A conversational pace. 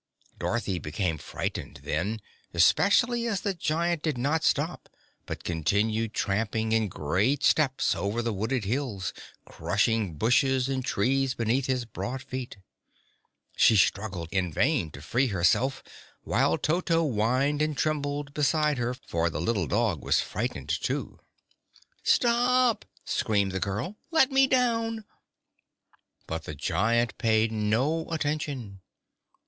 No: slow, 130 wpm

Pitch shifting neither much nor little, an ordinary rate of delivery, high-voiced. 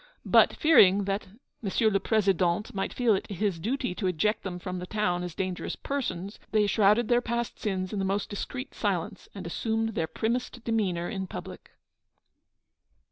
Yes: average, 3.3 semitones; average, 170 wpm; high, 205 Hz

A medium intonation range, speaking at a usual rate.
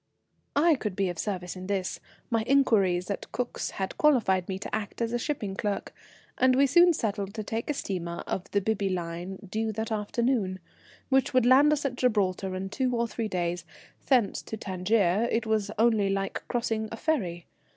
Yes: average, 4.2 semitones; average, 185 wpm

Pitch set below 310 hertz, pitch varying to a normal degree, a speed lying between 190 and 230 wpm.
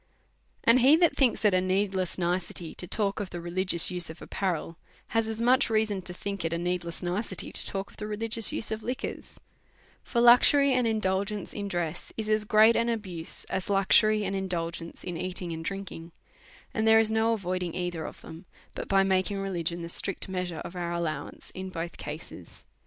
Yes: high, 190 Hz; average, 3.7 semitones; average, 200 wpm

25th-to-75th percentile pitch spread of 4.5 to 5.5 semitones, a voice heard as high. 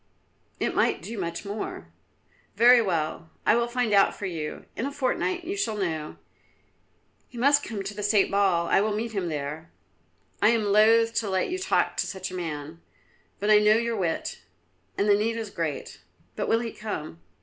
Yes: average, 4.9 semitones; high, 205 Hz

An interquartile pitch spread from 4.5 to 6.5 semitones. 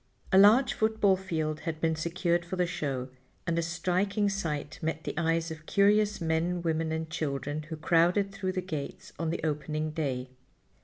No: average, 3.1 semitones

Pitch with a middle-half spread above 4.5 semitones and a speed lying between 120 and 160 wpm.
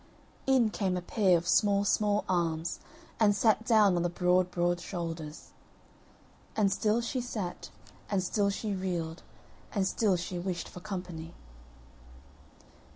No: average, 3.1 semitones; average, 140 wpm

